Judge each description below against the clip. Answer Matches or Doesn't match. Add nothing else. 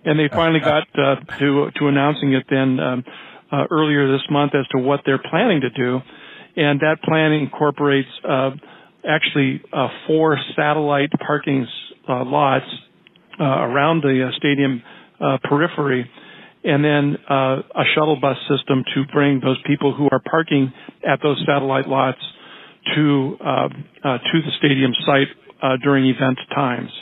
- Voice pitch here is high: Doesn't match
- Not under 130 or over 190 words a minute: Matches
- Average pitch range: Doesn't match